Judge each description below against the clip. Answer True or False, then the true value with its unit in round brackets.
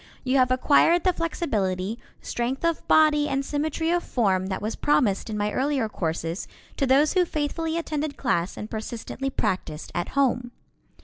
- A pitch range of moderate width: False (6.4 semitones)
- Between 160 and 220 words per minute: True (165 wpm)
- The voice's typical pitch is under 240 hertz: False (265 Hz)